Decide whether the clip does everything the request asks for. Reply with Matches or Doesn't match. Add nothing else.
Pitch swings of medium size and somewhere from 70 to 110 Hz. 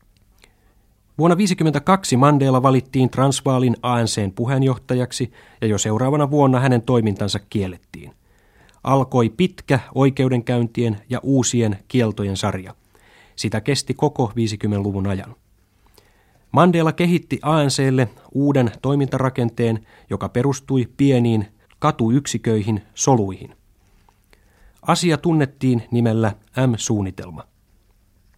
Doesn't match